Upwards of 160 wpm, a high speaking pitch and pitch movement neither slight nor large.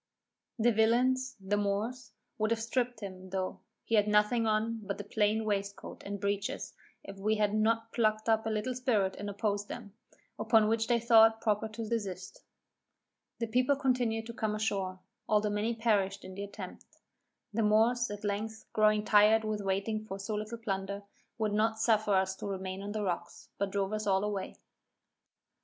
No: average, 180 wpm; high, 215 Hz; narrow, 1.9 semitones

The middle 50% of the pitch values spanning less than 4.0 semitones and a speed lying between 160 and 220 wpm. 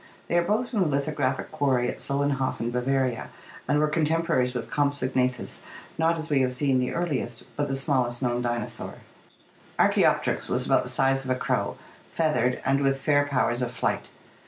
Yes: average, 2.9 semitones; average, 175 wpm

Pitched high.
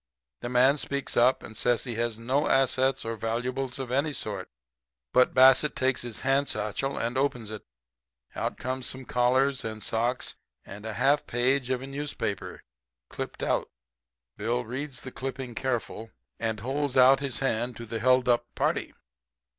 No: low, 125 Hz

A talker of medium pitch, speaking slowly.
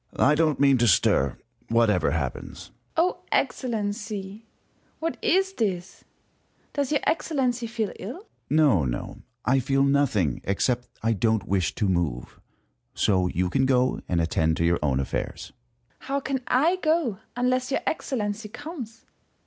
No: medium, 155 Hz; average, 160 wpm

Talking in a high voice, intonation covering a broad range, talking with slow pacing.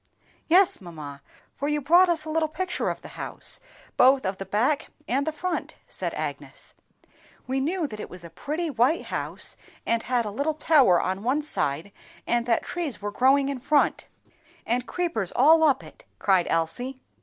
No: very high, 265 Hz; wide, 6.9 semitones; average, 180 wpm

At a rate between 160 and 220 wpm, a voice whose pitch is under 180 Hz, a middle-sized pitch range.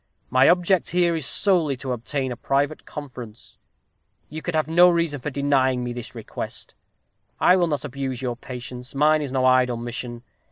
Yes: average, 175 wpm; low, 135 Hz; average, 3.8 semitones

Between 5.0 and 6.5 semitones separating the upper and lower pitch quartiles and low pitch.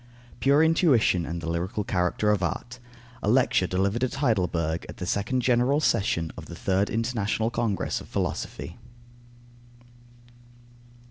Yes: wide, 5.4 semitones; low, 105 Hz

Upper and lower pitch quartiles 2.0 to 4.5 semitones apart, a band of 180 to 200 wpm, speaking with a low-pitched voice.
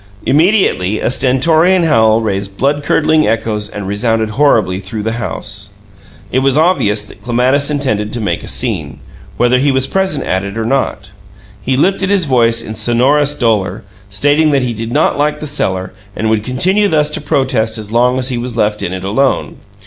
No: average, 5.1 semitones; average, 185 wpm; low, 120 Hz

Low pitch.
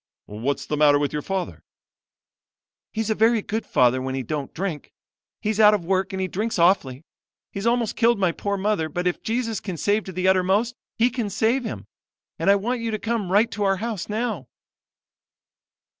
No: high, 200 Hz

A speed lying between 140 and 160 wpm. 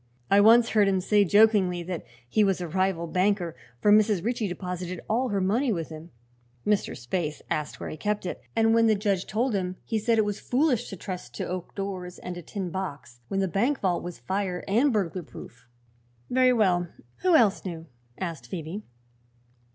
No: average, 195 wpm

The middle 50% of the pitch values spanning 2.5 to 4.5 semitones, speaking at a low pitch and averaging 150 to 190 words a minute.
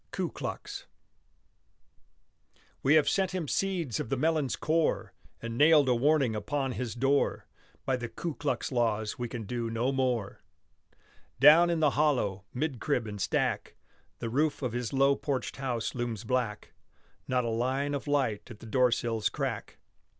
Yes: average, 3.9 semitones; low, 130 Hz; average, 160 wpm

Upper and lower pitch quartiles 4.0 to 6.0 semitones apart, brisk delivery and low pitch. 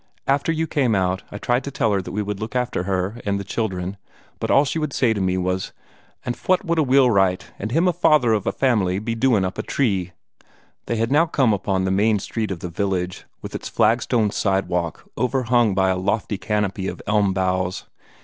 Yes: average, 4.7 semitones; fast, 220 wpm; low, 105 Hz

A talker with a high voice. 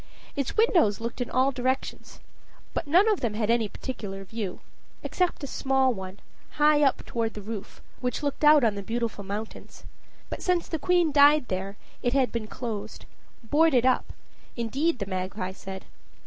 Yes: high, 240 Hz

